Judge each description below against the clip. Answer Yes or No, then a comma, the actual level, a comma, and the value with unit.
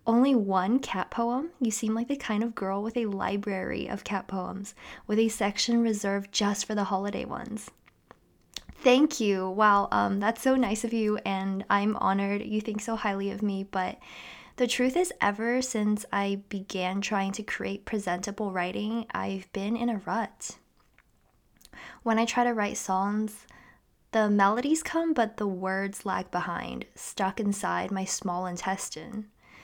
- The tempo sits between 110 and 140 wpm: No, average, 165 wpm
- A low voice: No, high, 210 Hz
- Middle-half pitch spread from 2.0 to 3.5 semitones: Yes, average, 2.9 semitones